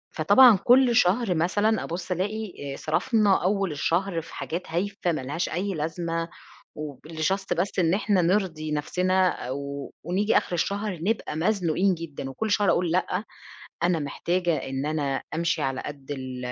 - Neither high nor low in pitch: Yes, medium, 175 Hz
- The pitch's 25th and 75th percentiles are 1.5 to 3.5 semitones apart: No, average, 4.3 semitones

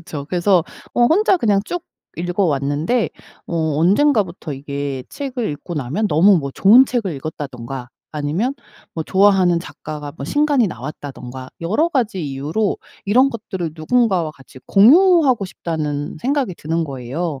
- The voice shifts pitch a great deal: Yes, wide, 7.6 semitones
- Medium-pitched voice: Yes, medium, 175 Hz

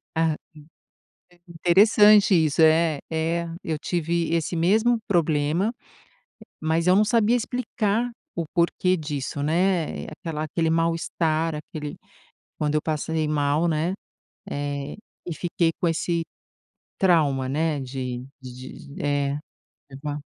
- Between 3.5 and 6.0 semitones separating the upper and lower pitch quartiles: No, average, 2.8 semitones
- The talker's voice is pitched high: No, medium, 160 Hz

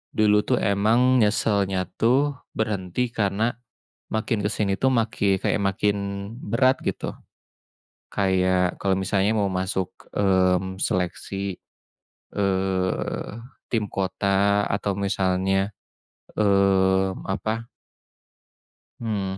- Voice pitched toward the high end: No, low, 100 Hz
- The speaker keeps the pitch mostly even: Yes, narrow, 2.2 semitones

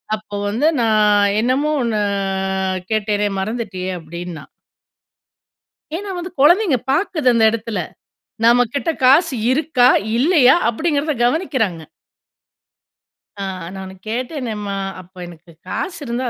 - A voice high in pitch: Yes, high, 235 Hz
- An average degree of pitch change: No, wide, 5.7 semitones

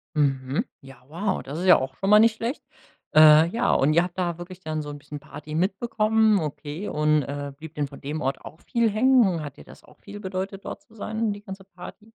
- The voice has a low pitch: No, medium, 175 Hz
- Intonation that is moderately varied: No, wide, 5.7 semitones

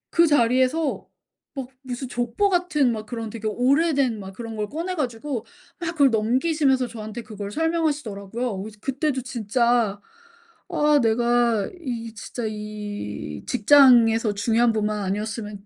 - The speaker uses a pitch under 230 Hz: No, high, 240 Hz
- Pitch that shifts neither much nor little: Yes, average, 4.5 semitones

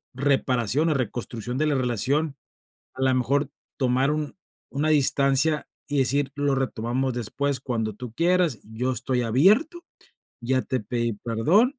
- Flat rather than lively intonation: No, average, 3.1 semitones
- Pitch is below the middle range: Yes, low, 130 Hz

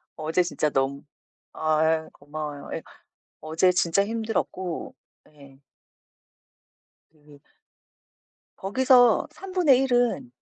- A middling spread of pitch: No, wide, 8.2 semitones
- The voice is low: No, medium, 175 Hz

